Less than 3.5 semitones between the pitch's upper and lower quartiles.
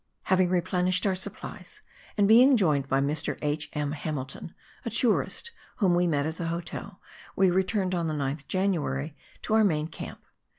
No: average, 4.1 semitones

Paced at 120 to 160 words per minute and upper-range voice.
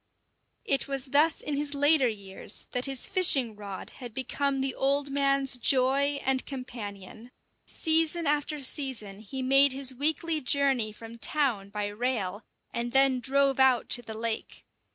Yes: average, 155 wpm; very high, 265 Hz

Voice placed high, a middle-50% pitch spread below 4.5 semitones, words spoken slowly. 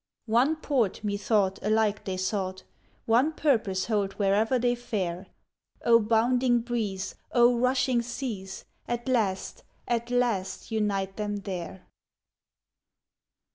Yes: high, 220 Hz; average, 3.7 semitones; slow, 110 wpm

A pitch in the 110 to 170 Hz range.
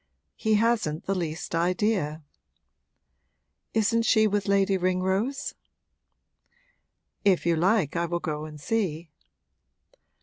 No: medium, 185 Hz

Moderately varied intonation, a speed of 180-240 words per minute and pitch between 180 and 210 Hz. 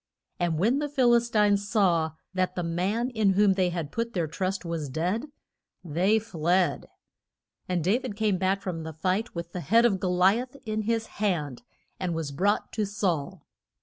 Yes: average, 4.2 semitones; average, 190 wpm; high, 190 Hz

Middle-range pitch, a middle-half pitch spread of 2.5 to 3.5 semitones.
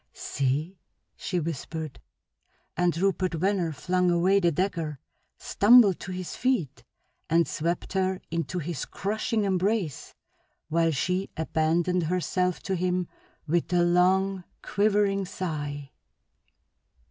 Yes: medium, 180 Hz; average, 2.8 semitones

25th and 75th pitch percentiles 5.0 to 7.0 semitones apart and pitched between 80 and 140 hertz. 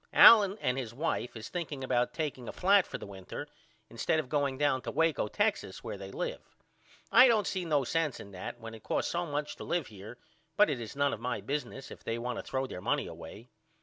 Yes: average, 5.3 semitones; low, 135 Hz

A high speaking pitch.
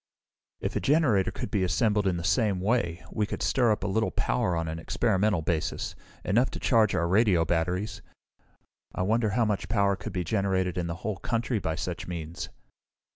No: low, 100 Hz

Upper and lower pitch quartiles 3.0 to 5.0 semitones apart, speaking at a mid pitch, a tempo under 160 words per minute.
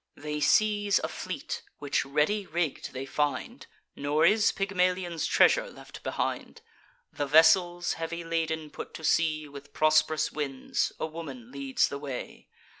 Yes: average, 3.3 semitones; medium, 155 Hz; average, 140 wpm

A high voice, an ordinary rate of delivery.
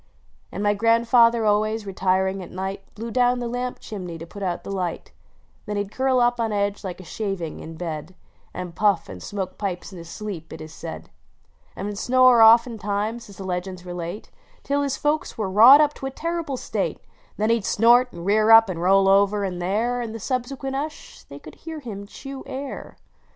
No: high, 210 Hz; fast, 215 wpm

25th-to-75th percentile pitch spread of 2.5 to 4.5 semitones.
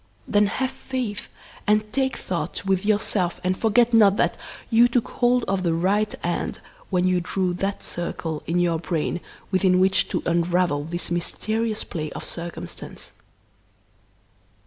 Yes: average, 3.7 semitones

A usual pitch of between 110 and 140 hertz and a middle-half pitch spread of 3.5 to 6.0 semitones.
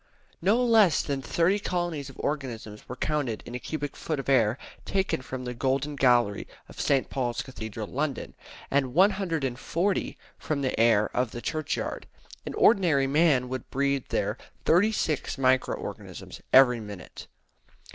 Yes: low, 135 Hz; average, 4.3 semitones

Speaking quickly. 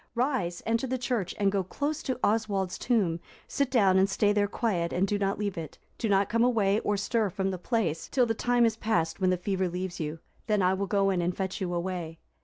Yes: fast, 235 wpm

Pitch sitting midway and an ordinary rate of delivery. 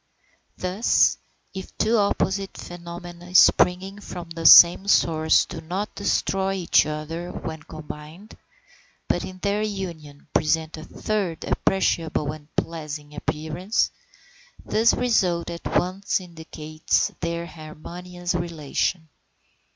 No: medium, 170 Hz; slow, 110 wpm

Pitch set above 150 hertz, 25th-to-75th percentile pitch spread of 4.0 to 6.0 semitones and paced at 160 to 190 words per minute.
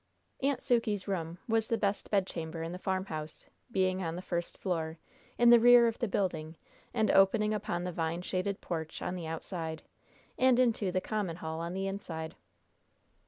Yes: medium, 185 Hz; average, 4.3 semitones; average, 175 wpm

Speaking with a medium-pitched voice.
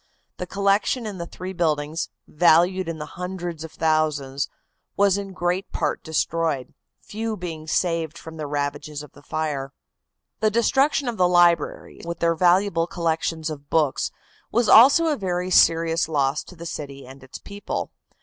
Yes: medium, 170 Hz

